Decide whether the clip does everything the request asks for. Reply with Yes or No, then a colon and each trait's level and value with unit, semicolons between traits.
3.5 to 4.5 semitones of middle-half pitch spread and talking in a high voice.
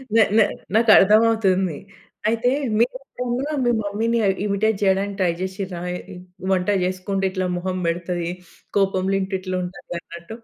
No: average, 2.8 semitones; high, 195 Hz